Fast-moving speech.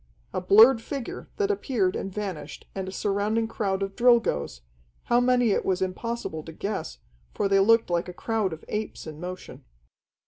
No: average, 175 wpm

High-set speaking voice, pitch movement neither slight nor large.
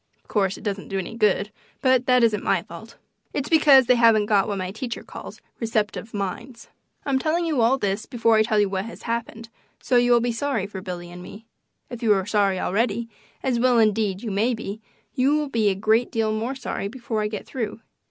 Yes: high, 225 Hz; average, 3.2 semitones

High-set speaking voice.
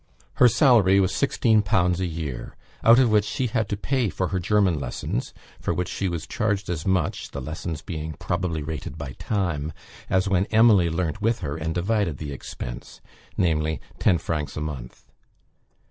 No: very low, 90 Hz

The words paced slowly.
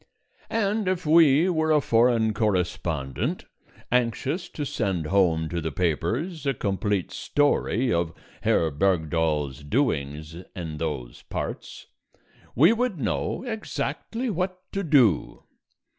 Yes: slow, 115 wpm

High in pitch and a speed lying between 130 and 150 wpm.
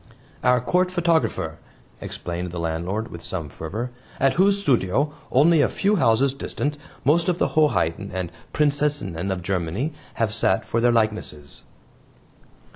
No: low, 120 Hz; average, 140 wpm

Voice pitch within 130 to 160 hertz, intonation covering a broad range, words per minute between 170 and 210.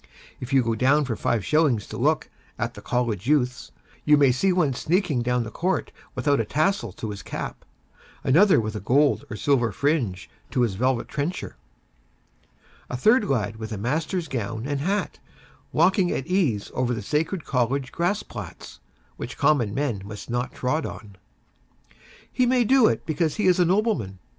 Yes: low, 135 Hz; wide, 6.2 semitones; average, 175 wpm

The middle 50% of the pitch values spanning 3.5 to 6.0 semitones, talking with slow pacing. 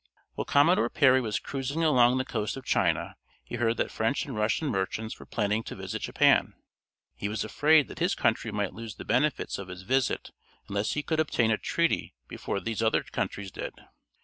No: average, 4.9 semitones; average, 195 wpm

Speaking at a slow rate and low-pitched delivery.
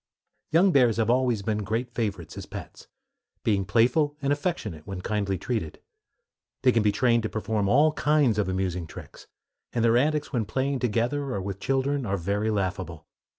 No: average, 175 wpm; low, 115 Hz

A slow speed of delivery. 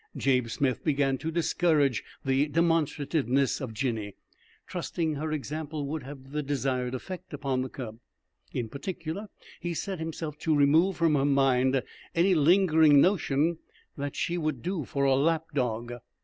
No: average, 150 wpm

